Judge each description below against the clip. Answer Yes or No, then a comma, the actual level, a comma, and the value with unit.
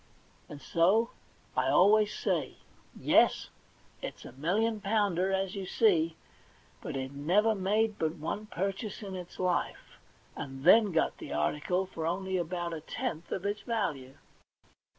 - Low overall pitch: No, medium, 185 Hz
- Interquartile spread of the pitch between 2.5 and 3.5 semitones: No, average, 4.3 semitones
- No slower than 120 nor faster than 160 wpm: Yes, average, 150 wpm